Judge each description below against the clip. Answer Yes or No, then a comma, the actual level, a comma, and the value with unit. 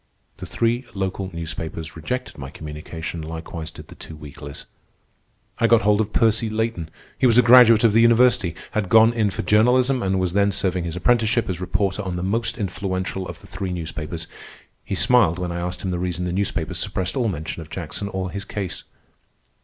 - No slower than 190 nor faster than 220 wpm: Yes, average, 195 wpm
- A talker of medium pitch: No, very low, 95 Hz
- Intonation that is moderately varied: Yes, average, 4.6 semitones